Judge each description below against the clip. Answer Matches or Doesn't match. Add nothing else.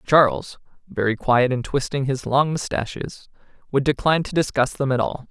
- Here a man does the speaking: Matches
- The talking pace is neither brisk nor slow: Matches